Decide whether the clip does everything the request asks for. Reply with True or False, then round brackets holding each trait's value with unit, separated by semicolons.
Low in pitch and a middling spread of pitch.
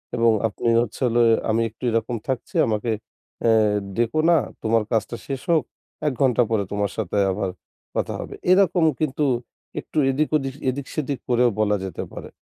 True (120 Hz; 3.7 semitones)